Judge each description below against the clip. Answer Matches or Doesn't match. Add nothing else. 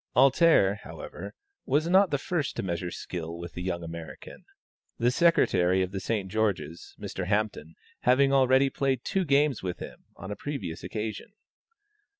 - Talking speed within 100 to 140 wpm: Doesn't match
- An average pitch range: Doesn't match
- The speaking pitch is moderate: Doesn't match